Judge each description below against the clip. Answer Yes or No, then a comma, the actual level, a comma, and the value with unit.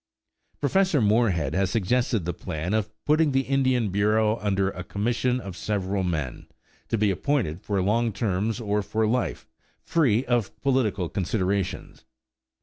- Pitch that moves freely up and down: No, average, 4.1 semitones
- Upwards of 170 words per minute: No, average, 145 wpm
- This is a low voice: Yes, low, 105 Hz